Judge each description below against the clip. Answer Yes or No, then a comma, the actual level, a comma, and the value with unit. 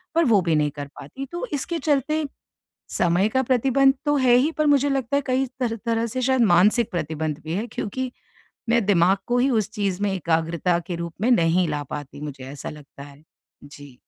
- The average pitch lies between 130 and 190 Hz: No, high, 205 Hz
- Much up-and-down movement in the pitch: Yes, wide, 8.2 semitones